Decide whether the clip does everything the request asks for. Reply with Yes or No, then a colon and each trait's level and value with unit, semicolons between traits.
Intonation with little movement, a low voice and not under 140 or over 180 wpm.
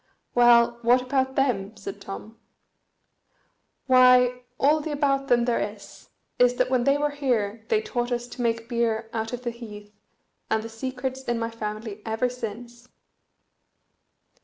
No: narrow, 2.3 semitones; high, 240 Hz; average, 155 wpm